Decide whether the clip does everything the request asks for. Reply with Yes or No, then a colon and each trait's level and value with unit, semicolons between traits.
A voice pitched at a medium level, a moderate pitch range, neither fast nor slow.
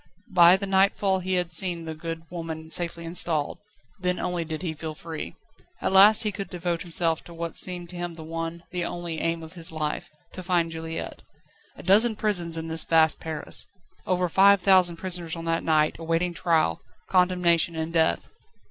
No: medium, 170 Hz; narrow, 1.8 semitones; average, 185 wpm